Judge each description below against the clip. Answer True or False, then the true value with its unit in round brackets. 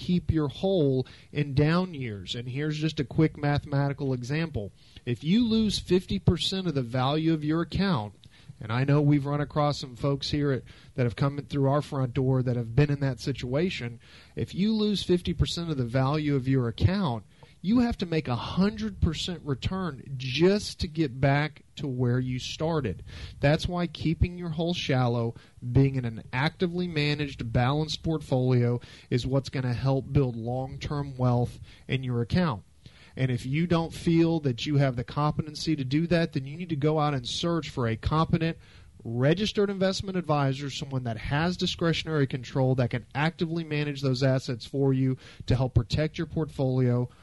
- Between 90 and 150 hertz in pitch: True (140 Hz)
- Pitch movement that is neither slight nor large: True (4.1 semitones)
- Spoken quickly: False (180 wpm)